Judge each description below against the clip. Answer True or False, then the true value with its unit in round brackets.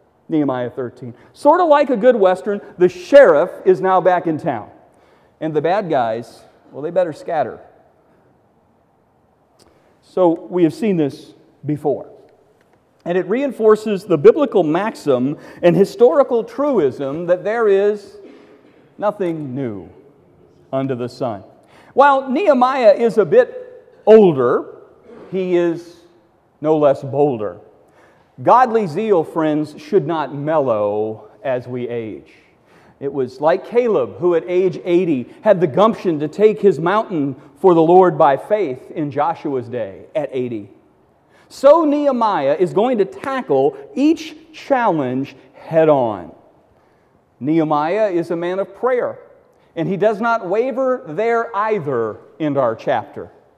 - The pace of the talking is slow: True (130 wpm)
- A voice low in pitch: False (185 Hz)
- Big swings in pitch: True (8.0 semitones)